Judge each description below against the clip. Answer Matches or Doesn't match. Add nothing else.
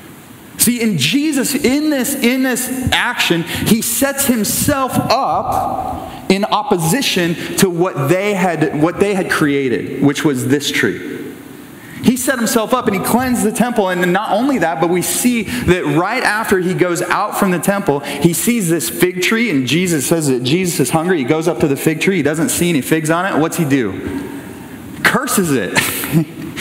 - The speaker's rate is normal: Matches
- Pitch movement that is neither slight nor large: Doesn't match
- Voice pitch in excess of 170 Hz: Matches